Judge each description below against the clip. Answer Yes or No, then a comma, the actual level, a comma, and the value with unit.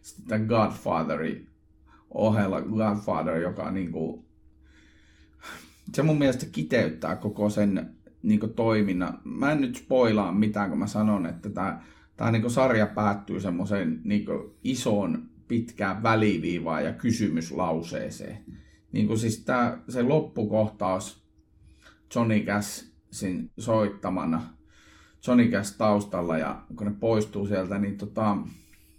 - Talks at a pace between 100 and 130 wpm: Yes, average, 110 wpm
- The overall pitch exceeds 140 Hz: No, low, 105 Hz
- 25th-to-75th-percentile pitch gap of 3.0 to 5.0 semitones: Yes, average, 4.3 semitones